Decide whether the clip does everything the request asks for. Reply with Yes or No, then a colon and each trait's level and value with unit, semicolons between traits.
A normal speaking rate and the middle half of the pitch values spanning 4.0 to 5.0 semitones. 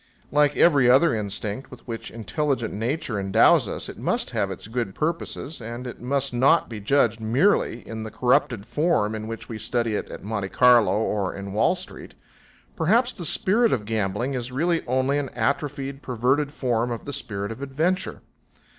Yes: average, 180 wpm; average, 4.6 semitones